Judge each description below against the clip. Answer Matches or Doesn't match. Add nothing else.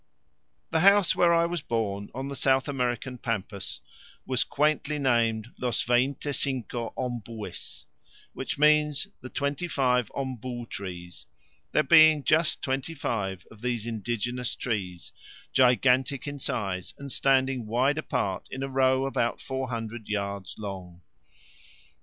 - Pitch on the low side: Matches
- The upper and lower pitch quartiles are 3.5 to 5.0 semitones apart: Matches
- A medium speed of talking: Doesn't match